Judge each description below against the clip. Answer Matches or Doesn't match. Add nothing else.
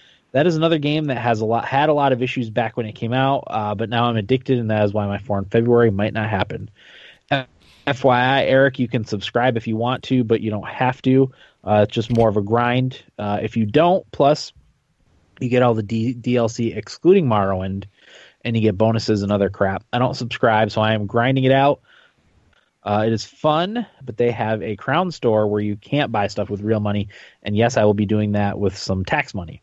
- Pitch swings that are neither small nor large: Matches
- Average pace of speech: Doesn't match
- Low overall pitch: Matches